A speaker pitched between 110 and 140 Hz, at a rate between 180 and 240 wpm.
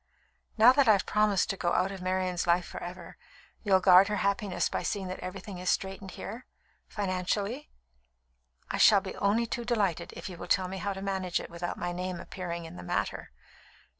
No: high, 190 Hz; average, 195 wpm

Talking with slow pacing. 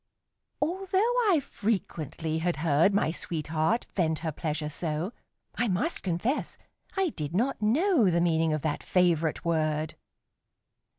Yes: slow, 130 wpm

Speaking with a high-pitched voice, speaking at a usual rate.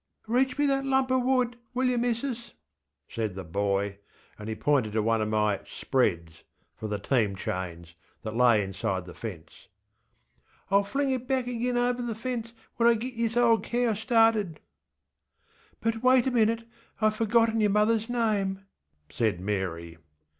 Yes: high, 210 Hz; average, 160 wpm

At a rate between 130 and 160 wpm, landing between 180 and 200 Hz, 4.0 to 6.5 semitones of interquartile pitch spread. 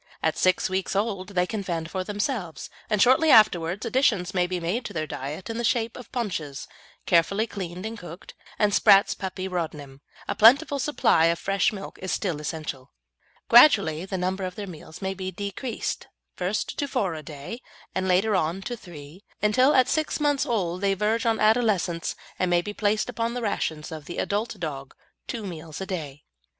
No: average, 190 wpm; high, 190 Hz; average, 4.6 semitones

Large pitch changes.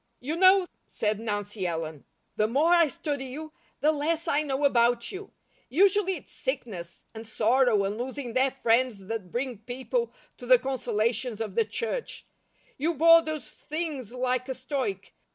Yes: wide, 5.7 semitones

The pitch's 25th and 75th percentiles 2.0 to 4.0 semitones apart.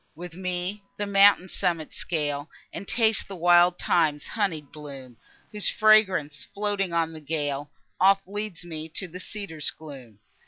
No: average, 4.5 semitones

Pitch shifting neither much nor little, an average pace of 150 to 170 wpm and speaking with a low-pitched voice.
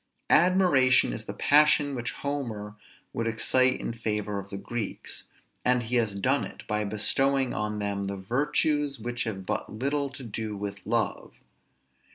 Yes: average, 4.7 semitones; average, 160 wpm; low, 115 Hz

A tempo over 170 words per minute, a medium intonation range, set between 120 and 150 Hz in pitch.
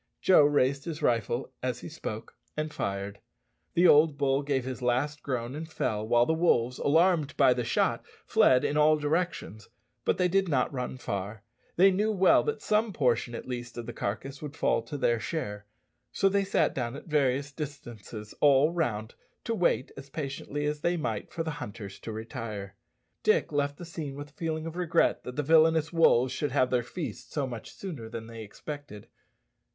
Yes: average, 190 wpm; average, 5.0 semitones; medium, 140 Hz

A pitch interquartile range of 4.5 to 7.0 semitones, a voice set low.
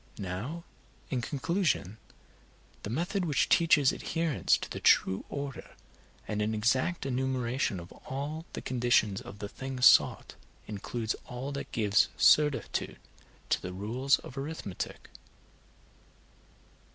Yes: average, 5.1 semitones; low, 130 Hz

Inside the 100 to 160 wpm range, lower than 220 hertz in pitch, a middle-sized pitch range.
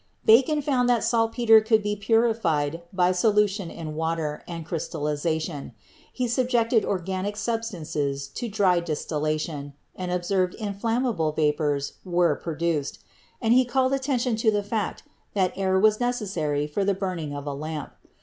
No: average, 150 wpm; high, 190 Hz; wide, 6.2 semitones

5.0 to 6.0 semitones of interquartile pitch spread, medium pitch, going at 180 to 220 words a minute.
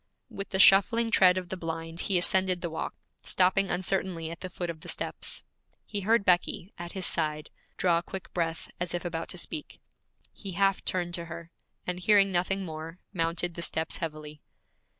No: narrow, 2.4 semitones; medium, 175 Hz; average, 190 wpm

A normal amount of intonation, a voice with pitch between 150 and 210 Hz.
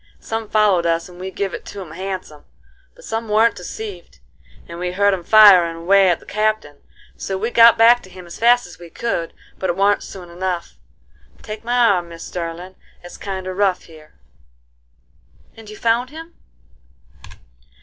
Yes: average, 3.8 semitones; high, 190 Hz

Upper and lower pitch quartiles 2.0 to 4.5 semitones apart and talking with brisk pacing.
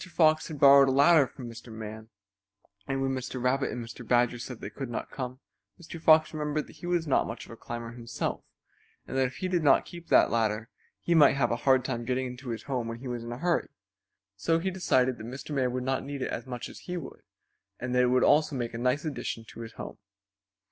Yes: average, 3.8 semitones; fast, 245 wpm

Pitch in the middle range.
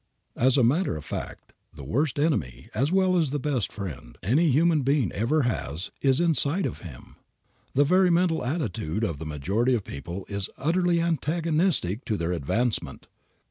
No: low, 130 Hz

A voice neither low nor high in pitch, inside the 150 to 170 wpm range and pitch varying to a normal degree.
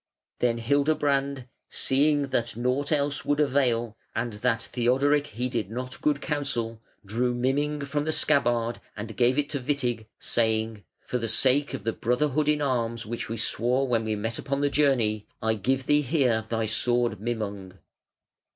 No: low, 125 Hz; average, 160 wpm; average, 3.8 semitones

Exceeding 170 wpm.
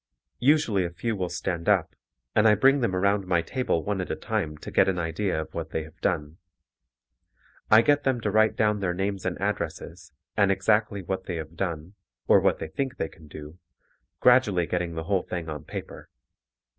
Yes: average, 200 wpm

